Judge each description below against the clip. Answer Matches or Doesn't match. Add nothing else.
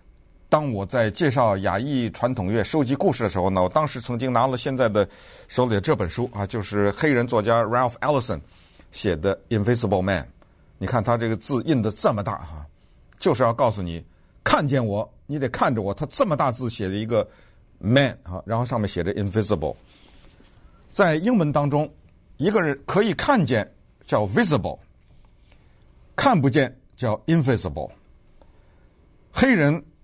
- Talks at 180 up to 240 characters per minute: Doesn't match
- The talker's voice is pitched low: Matches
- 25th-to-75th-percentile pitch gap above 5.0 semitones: Matches